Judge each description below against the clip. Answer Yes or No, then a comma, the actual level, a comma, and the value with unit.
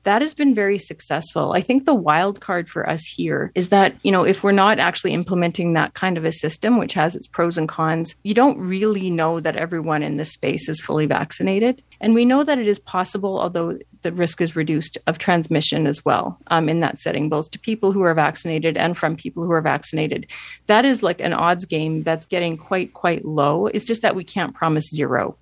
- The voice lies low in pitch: No, medium, 170 Hz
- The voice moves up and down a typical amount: Yes, average, 3.9 semitones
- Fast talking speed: Yes, fast, 225 wpm